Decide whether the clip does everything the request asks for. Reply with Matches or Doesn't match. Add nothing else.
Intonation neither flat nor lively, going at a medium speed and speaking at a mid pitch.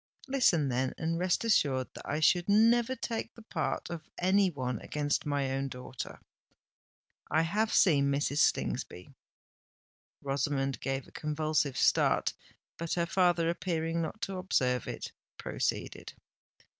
Doesn't match